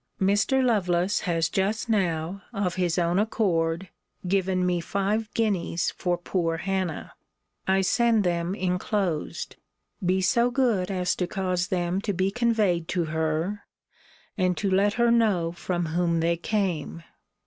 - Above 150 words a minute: No, average, 140 wpm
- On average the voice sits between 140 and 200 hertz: Yes, medium, 185 Hz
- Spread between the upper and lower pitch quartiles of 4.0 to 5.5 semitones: No, average, 2.9 semitones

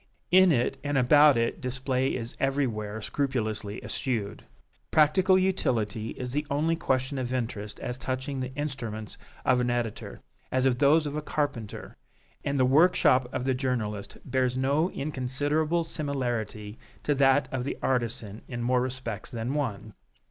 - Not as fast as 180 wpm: Yes, average, 150 wpm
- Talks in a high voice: No, low, 130 Hz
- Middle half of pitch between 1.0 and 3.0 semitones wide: No, average, 3.5 semitones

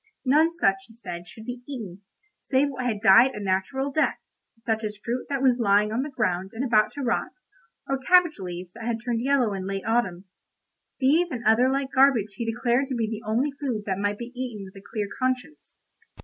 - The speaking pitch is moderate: No, high, 235 Hz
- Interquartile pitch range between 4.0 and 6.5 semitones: Yes, average, 4.4 semitones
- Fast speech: Yes, fast, 210 wpm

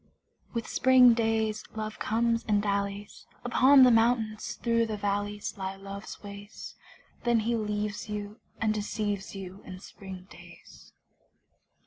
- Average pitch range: No, narrow, 2.2 semitones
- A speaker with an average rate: No, slow, 130 wpm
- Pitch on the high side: Yes, high, 210 Hz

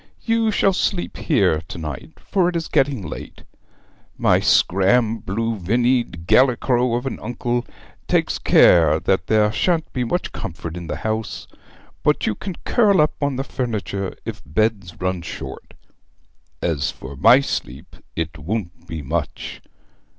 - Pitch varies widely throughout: Yes, wide, 7.1 semitones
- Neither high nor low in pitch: No, low, 110 Hz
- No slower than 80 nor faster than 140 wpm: No, average, 150 wpm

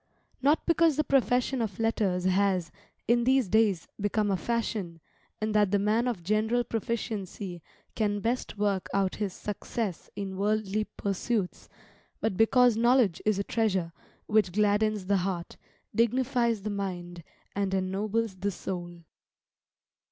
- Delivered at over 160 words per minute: No, slow, 135 wpm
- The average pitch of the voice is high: Yes, high, 210 Hz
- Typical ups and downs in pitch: Yes, average, 3.1 semitones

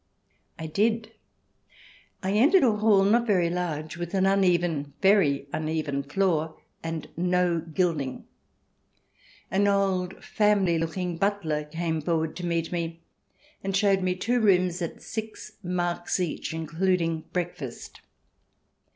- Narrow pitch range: No, average, 3.3 semitones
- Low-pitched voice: No, medium, 175 Hz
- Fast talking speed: No, slow, 135 wpm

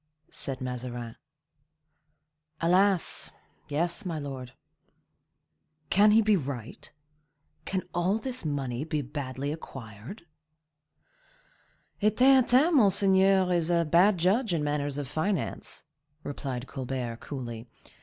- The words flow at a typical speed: No, slow, 105 wpm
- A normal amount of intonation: No, wide, 6.7 semitones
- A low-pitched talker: No, medium, 155 Hz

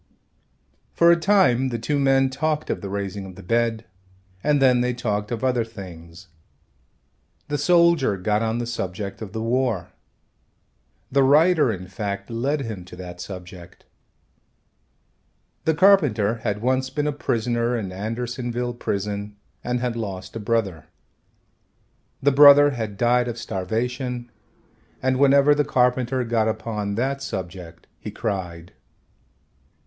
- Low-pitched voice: Yes, low, 115 Hz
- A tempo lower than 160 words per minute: Yes, average, 140 wpm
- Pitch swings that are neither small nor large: Yes, average, 4.7 semitones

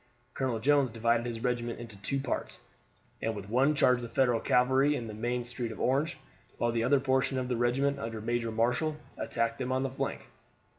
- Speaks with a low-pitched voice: Yes, low, 120 Hz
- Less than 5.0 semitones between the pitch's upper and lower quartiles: Yes, narrow, 2.4 semitones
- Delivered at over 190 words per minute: Yes, average, 200 wpm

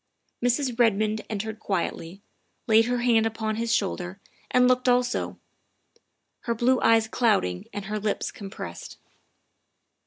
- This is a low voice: No, high, 220 Hz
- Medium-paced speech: No, slow, 130 wpm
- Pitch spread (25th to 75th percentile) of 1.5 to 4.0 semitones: Yes, average, 2.9 semitones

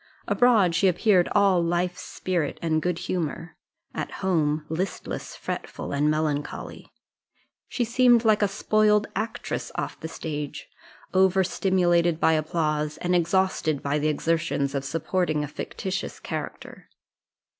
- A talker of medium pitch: Yes, medium, 175 Hz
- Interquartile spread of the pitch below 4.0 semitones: Yes, average, 3.6 semitones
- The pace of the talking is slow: Yes, slow, 130 wpm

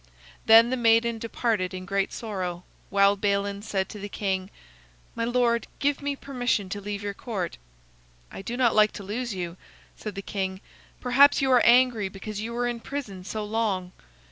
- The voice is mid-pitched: No, high, 215 Hz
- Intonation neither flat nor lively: Yes, average, 3.3 semitones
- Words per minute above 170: Yes, average, 180 wpm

